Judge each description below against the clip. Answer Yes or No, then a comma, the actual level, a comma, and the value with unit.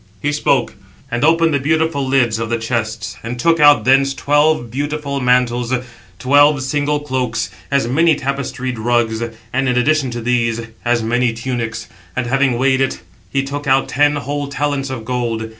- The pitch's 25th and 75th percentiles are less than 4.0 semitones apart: Yes, average, 3.3 semitones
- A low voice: Yes, low, 130 Hz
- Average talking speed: Yes, average, 170 wpm